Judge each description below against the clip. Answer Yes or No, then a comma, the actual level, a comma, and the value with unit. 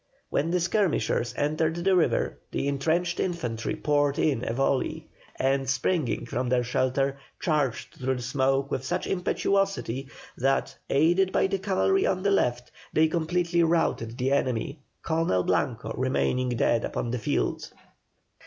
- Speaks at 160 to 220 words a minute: No, average, 145 wpm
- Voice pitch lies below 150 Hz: Yes, medium, 140 Hz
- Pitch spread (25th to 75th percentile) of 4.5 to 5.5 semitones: Yes, average, 5.1 semitones